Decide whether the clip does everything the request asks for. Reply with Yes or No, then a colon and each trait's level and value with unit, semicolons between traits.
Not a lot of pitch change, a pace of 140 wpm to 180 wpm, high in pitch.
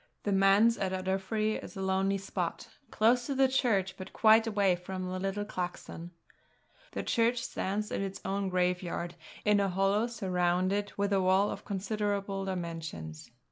Yes: narrow, 2.1 semitones; average, 160 wpm; high, 195 Hz